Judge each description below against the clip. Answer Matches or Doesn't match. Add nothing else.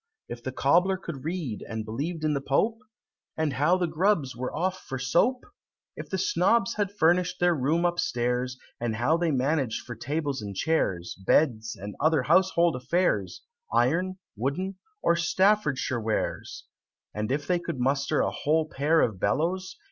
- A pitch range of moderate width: Doesn't match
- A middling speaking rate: Matches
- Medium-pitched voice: Matches